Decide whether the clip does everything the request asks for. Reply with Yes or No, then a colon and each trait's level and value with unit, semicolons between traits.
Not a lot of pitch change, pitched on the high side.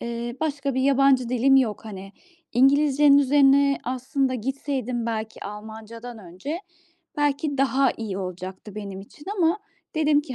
No: average, 4.1 semitones; very high, 260 Hz